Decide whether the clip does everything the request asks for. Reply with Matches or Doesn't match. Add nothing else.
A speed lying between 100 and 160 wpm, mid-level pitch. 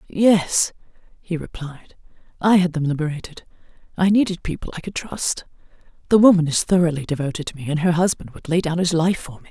Doesn't match